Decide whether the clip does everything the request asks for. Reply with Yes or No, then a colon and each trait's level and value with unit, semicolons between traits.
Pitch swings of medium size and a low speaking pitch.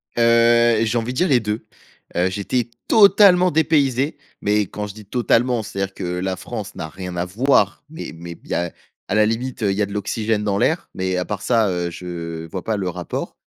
Yes: average, 4.4 semitones; low, 105 Hz